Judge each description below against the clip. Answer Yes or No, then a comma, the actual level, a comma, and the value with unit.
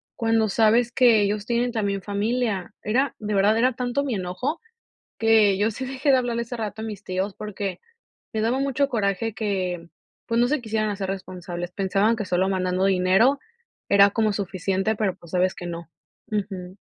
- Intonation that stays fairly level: No, average, 3.4 semitones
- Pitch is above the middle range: Yes, high, 210 Hz